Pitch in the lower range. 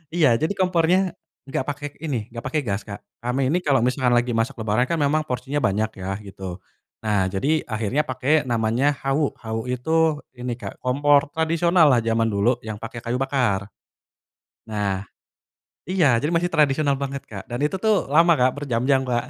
Yes: low, 130 Hz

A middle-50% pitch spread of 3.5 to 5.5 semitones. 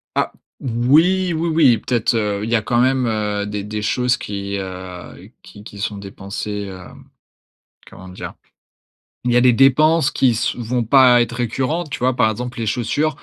Yes: average, 4.1 semitones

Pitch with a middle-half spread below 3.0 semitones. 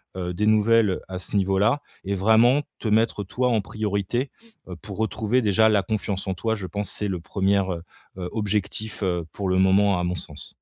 Yes: narrow, 2.5 semitones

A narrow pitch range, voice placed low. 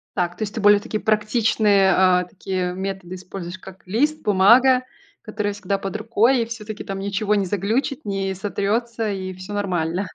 No: narrow, 2.3 semitones; high, 200 Hz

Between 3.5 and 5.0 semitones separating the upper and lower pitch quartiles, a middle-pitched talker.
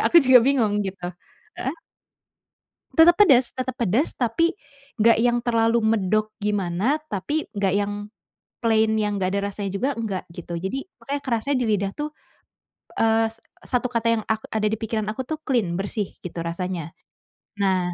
No: average, 4.0 semitones; high, 220 Hz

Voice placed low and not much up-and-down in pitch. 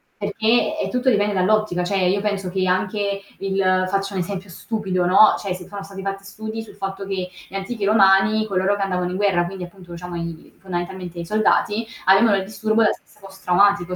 No: high, 195 Hz; narrow, 2.0 semitones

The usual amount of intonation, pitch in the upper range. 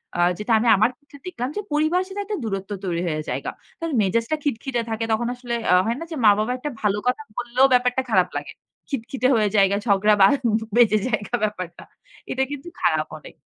Yes: average, 4.3 semitones; high, 235 Hz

